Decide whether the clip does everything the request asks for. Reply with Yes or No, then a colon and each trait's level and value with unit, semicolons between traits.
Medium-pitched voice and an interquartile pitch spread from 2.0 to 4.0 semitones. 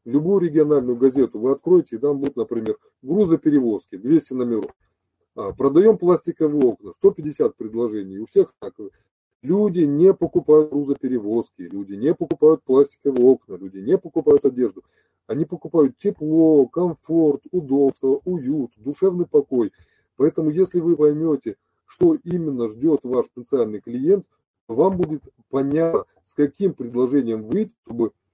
No: medium, 150 Hz; average, 5.2 semitones